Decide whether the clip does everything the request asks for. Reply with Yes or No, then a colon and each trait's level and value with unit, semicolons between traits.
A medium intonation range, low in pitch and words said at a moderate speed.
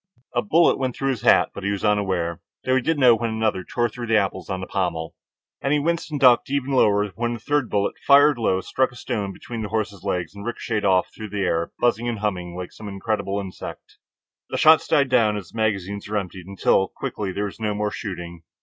No: average, 3.8 semitones; low, 105 Hz; fast, 230 wpm